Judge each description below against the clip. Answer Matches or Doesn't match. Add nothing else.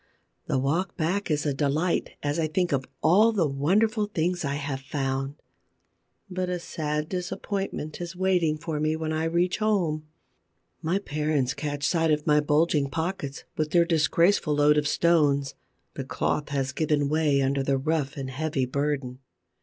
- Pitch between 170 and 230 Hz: Doesn't match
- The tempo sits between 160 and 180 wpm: Matches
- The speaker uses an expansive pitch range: Doesn't match